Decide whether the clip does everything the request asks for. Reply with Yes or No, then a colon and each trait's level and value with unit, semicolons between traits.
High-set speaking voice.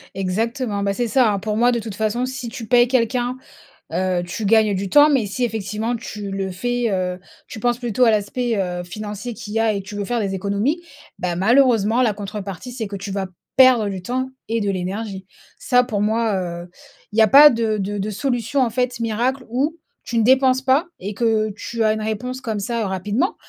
Yes: high, 220 Hz